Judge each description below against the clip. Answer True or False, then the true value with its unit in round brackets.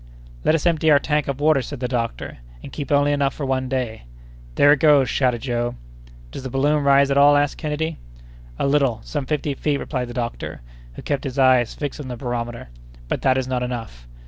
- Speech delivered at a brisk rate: True (210 wpm)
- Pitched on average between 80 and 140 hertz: True (135 Hz)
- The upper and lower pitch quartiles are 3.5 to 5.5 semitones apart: False (2.7 semitones)